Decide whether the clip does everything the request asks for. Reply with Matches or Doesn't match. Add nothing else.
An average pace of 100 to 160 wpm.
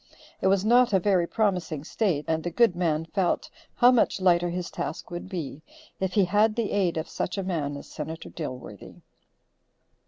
Doesn't match